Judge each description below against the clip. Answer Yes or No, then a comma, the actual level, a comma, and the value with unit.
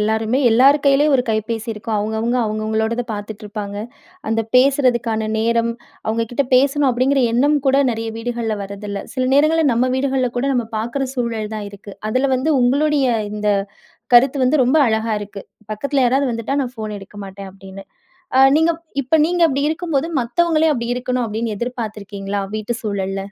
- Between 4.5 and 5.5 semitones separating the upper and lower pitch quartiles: No, average, 3.8 semitones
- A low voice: No, high, 235 Hz